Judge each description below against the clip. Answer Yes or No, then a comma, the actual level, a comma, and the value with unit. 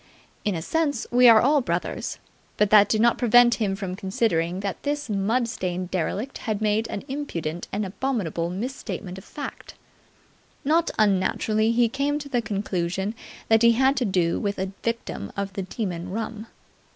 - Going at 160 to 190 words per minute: Yes, average, 175 wpm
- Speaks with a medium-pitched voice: No, high, 215 Hz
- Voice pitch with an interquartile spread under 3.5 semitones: No, average, 4.3 semitones